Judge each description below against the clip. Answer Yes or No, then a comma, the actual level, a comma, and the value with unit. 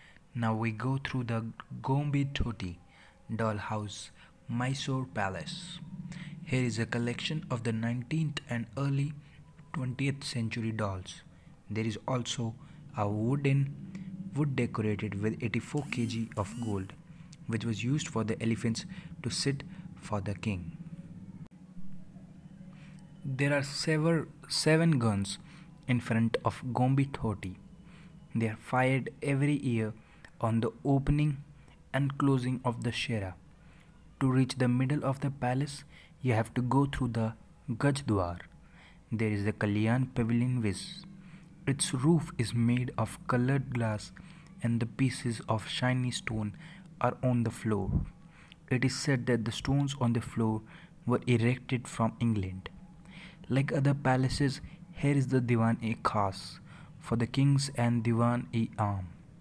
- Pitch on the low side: Yes, low, 130 Hz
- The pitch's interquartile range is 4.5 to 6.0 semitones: Yes, average, 4.9 semitones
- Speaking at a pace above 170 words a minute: No, slow, 135 wpm